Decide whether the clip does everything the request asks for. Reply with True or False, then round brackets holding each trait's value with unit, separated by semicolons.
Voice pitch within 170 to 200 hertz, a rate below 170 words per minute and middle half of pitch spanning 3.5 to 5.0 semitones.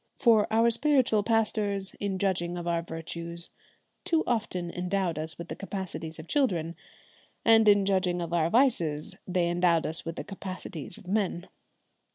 True (185 Hz; 160 wpm; 3.9 semitones)